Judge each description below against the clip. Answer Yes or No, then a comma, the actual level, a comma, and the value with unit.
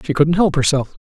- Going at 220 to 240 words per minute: Yes, fast, 235 wpm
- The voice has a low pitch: No, medium, 150 Hz